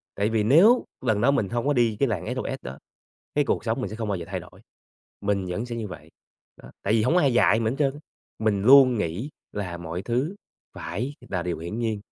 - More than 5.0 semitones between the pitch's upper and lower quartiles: No, average, 4.5 semitones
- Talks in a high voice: No, low, 110 Hz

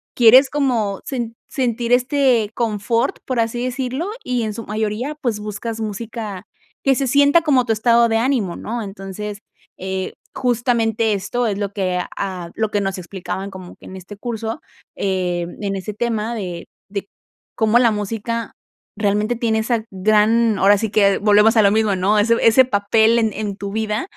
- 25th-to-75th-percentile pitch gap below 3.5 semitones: Yes, average, 2.8 semitones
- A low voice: No, high, 220 Hz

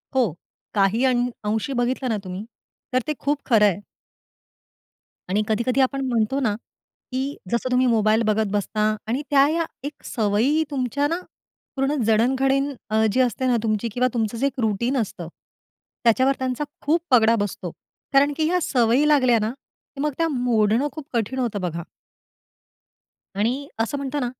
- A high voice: Yes, high, 245 Hz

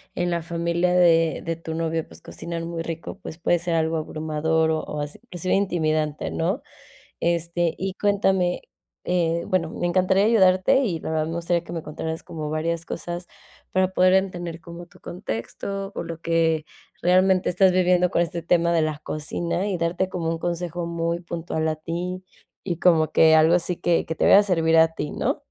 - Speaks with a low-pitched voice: No, medium, 170 Hz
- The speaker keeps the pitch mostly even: Yes, narrow, 1.8 semitones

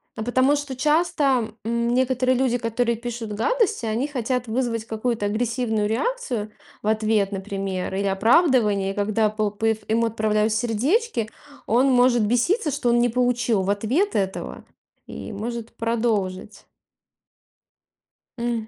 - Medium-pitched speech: No, high, 230 Hz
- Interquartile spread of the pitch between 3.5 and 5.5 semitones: No, average, 2.8 semitones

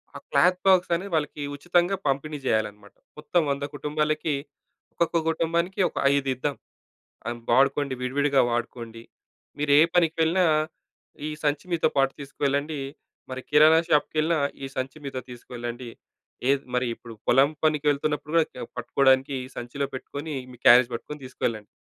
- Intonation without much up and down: No, average, 3.3 semitones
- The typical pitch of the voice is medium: Yes, medium, 145 Hz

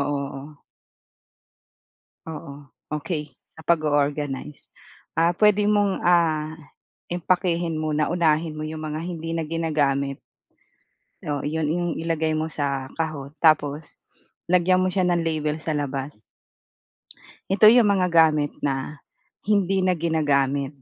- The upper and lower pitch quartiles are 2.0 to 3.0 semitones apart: Yes, average, 2.7 semitones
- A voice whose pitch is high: No, medium, 155 Hz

